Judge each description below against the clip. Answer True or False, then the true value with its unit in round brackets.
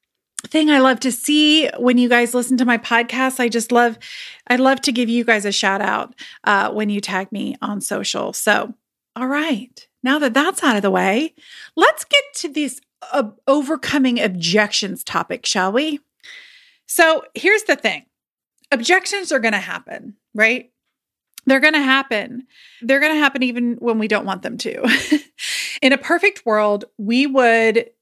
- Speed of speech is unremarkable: True (175 wpm)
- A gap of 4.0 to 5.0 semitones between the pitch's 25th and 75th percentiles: True (4.5 semitones)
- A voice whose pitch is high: True (255 Hz)